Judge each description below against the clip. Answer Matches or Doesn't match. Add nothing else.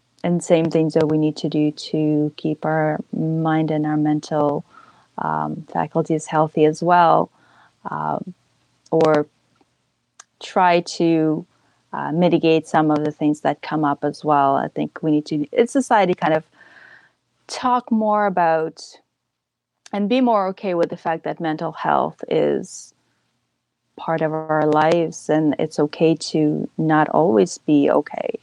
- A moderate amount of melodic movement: Doesn't match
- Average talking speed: Matches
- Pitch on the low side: Doesn't match